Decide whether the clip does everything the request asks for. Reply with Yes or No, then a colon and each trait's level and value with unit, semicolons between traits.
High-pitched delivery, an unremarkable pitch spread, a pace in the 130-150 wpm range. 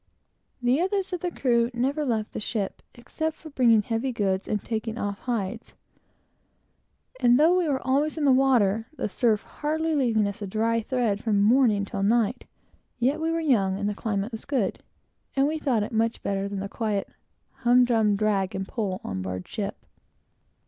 No: high, 230 Hz; average, 4.7 semitones; average, 185 wpm